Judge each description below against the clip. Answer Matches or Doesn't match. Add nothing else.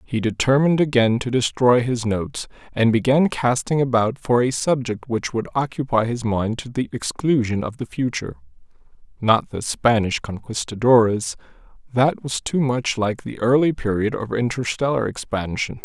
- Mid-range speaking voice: Doesn't match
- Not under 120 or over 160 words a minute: Matches